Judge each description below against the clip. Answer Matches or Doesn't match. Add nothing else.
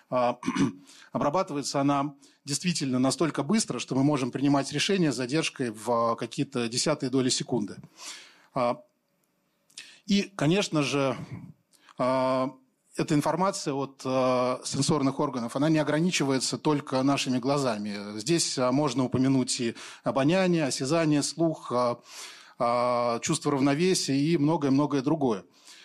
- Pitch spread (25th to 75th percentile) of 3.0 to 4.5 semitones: Matches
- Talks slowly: Matches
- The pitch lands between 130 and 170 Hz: Matches